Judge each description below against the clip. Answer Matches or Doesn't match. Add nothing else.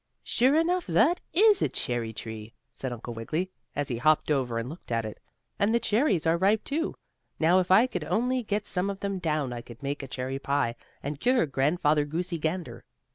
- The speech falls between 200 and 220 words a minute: Matches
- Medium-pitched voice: Matches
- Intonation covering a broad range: Matches